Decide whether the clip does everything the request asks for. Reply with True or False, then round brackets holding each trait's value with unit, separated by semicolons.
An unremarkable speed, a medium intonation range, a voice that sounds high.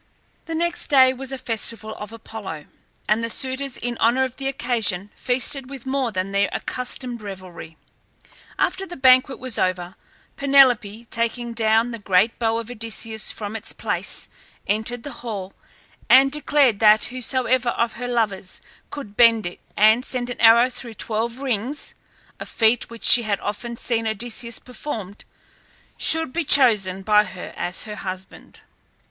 True (155 wpm; 3.3 semitones; 230 Hz)